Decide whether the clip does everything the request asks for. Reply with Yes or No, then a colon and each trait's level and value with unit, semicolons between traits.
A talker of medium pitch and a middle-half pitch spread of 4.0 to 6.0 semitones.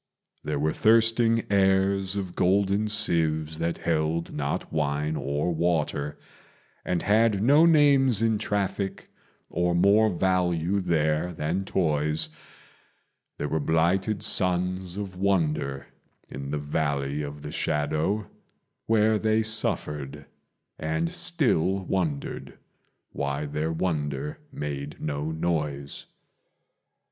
No: very low, 85 Hz; average, 4.7 semitones